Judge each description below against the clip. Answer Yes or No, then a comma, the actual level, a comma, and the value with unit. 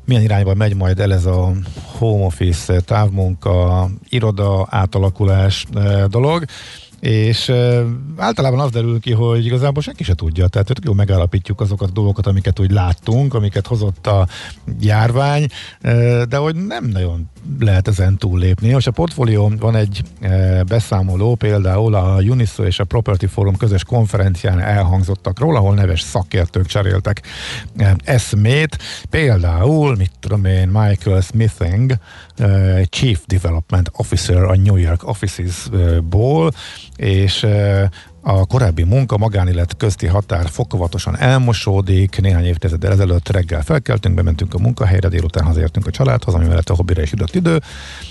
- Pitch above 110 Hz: No, low, 100 Hz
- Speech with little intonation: No, average, 3.8 semitones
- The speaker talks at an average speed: Yes, average, 135 wpm